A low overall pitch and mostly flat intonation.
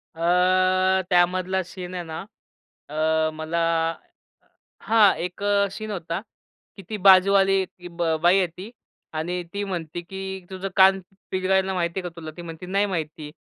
No: medium, 180 Hz; narrow, 2.3 semitones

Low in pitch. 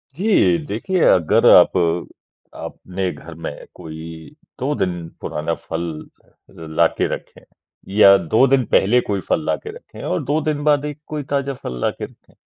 Yes: low, 100 Hz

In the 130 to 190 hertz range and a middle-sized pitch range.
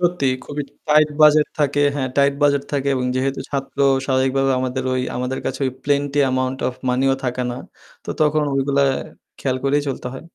No: low, 135 Hz; narrow, 1.8 semitones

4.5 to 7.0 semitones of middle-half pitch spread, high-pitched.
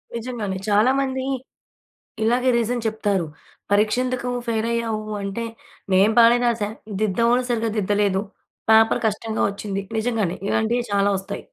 No: narrow, 2.6 semitones; high, 220 Hz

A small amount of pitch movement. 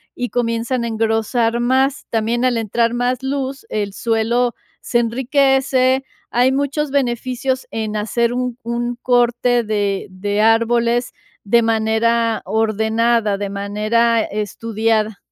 Yes: narrow, 2.0 semitones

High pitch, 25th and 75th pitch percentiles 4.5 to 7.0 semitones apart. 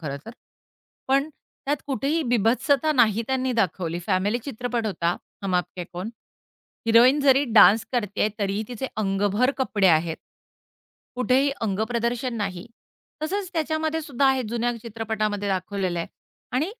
Yes: high, 230 Hz; average, 5.1 semitones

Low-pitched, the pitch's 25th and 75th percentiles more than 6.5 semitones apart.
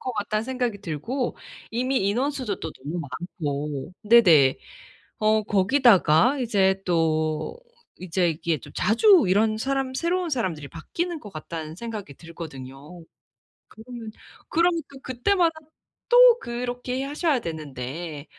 No: high, 215 Hz; wide, 8.1 semitones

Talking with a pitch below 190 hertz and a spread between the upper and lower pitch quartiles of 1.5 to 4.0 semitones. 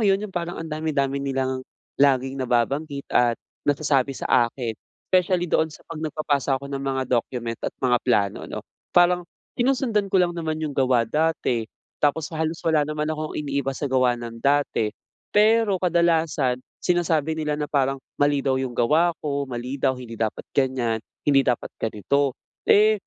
Yes: medium, 140 Hz; average, 3.7 semitones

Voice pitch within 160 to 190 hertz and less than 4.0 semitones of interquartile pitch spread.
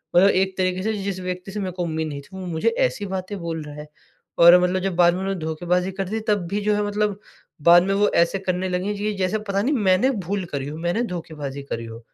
Yes: medium, 185 Hz; average, 2.8 semitones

